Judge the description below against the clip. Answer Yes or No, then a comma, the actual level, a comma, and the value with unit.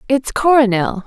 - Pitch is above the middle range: Yes, high, 245 Hz